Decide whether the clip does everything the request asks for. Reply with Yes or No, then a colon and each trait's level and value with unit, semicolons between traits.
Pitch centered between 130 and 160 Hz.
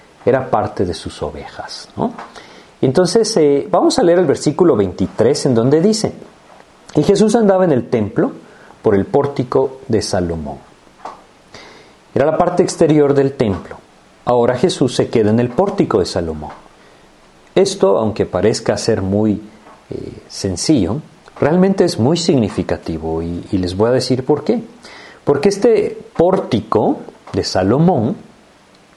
Yes: low, 135 Hz